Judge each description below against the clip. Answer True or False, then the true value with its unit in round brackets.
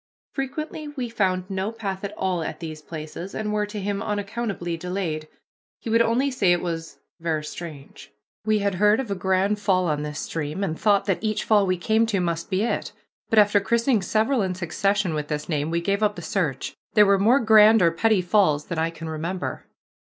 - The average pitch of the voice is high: True (195 Hz)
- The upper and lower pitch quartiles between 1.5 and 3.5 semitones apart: False (4.2 semitones)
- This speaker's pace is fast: True (210 wpm)